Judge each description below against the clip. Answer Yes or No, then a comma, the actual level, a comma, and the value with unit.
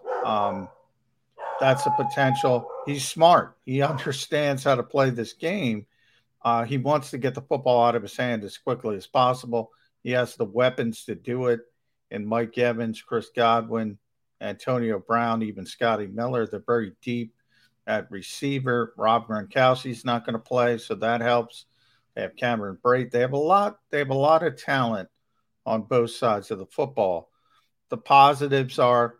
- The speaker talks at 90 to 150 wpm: No, average, 165 wpm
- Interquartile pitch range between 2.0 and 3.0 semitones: Yes, narrow, 2.6 semitones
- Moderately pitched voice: No, low, 125 Hz